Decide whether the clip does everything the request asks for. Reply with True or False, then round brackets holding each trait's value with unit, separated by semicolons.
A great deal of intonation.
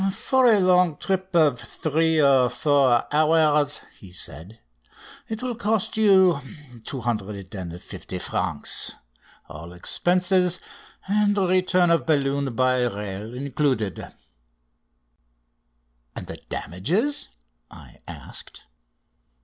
True (7.5 semitones)